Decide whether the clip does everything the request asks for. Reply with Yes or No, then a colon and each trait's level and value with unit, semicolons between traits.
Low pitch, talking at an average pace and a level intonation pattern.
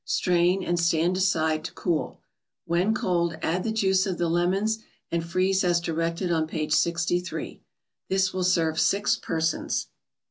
No: medium, 175 Hz; average, 150 wpm; narrow, 2.1 semitones